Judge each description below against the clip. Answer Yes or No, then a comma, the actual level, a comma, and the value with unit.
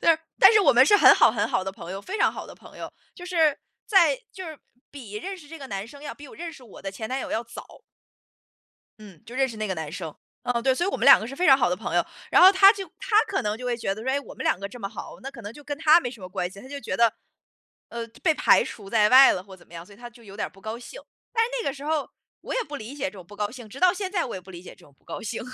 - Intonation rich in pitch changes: Yes, wide, 6.9 semitones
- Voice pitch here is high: Yes, high, 245 Hz